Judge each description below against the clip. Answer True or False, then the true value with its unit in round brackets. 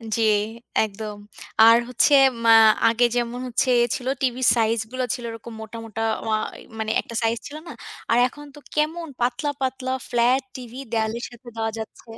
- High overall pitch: True (240 Hz)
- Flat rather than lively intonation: True (2.3 semitones)